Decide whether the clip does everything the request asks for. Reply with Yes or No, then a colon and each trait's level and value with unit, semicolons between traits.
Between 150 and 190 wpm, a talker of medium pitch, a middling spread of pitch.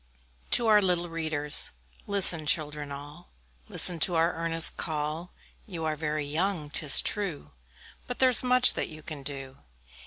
Yes: average, 155 wpm; medium, 160 Hz; average, 3.3 semitones